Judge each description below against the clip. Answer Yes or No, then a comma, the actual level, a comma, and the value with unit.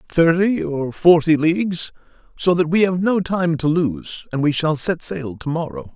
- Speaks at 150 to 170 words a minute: No, average, 190 wpm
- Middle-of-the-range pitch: Yes, medium, 165 Hz